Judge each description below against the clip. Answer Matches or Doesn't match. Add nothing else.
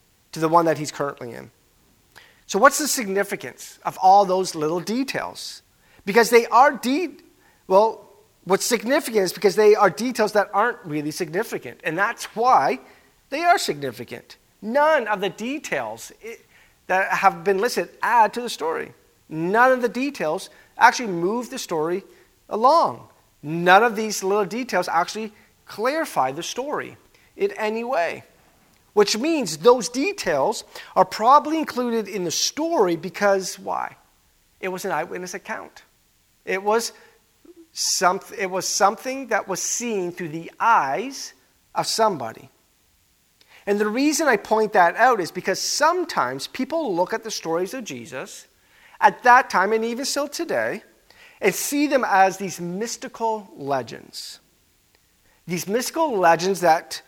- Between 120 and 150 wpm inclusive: Matches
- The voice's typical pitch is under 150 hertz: Doesn't match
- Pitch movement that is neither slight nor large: Doesn't match